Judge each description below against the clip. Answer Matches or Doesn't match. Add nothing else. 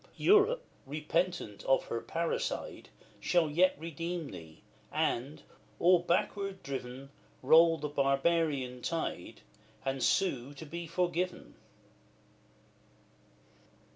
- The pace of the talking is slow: Matches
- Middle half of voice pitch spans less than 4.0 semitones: Doesn't match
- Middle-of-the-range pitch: Matches